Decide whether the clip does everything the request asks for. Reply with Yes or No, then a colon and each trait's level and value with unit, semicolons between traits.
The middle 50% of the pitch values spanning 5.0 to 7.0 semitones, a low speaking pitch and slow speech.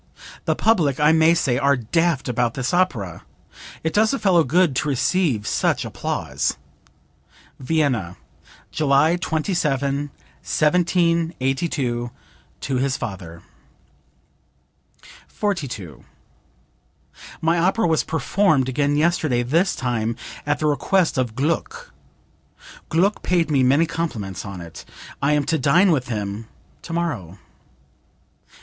No: wide, 5.4 semitones; medium, 145 Hz; slow, 115 wpm